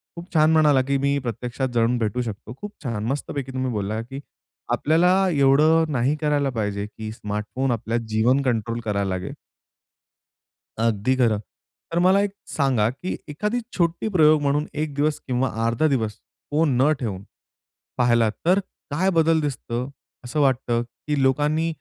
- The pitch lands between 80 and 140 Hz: Yes, low, 135 Hz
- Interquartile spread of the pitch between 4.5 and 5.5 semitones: Yes, average, 4.8 semitones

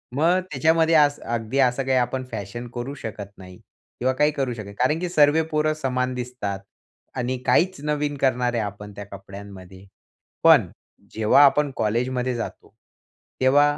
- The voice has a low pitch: Yes, low, 125 Hz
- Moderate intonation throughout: Yes, average, 5.0 semitones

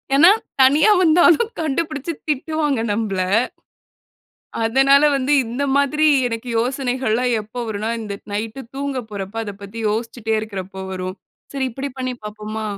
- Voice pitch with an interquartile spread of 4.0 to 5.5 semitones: Yes, average, 4.6 semitones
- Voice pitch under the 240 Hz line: No, high, 245 Hz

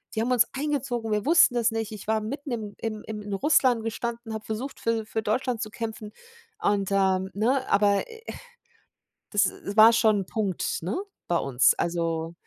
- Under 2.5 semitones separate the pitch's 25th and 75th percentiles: No, average, 2.8 semitones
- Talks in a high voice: Yes, high, 220 Hz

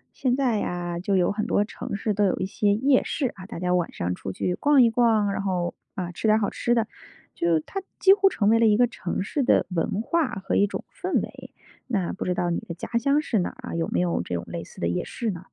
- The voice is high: Yes, high, 205 Hz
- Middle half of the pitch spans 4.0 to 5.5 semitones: Yes, average, 5.2 semitones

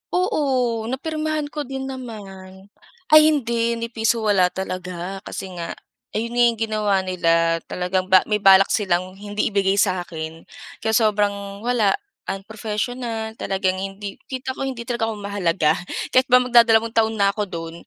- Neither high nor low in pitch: No, high, 210 Hz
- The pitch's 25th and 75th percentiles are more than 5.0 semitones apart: No, average, 3.7 semitones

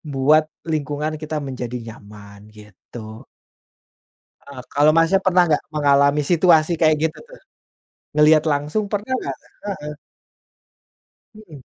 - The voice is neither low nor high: Yes, medium, 150 Hz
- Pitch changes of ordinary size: Yes, average, 3.0 semitones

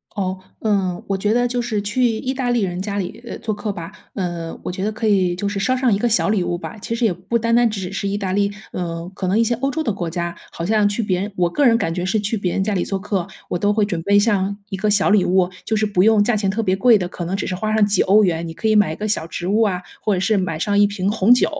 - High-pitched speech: Yes, high, 200 Hz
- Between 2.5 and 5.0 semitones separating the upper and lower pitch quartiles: Yes, average, 2.9 semitones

